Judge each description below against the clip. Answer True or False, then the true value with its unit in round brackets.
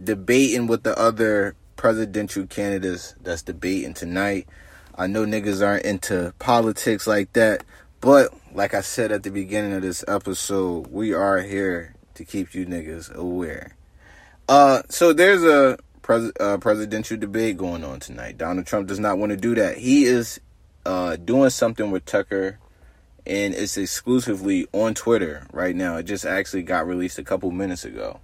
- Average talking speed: True (165 wpm)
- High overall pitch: False (100 Hz)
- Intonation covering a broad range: False (3.4 semitones)